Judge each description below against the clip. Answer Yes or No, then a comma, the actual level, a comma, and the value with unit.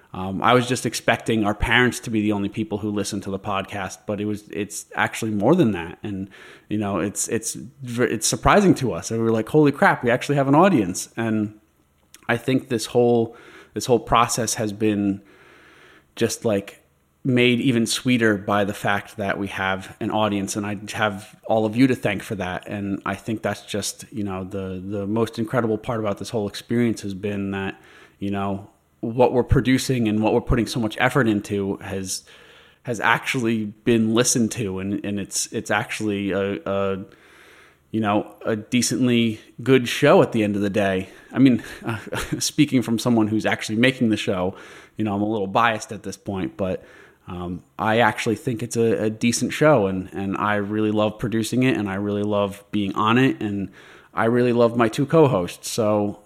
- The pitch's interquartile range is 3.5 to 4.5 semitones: No, average, 2.9 semitones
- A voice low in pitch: Yes, low, 110 Hz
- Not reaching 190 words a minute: No, average, 200 wpm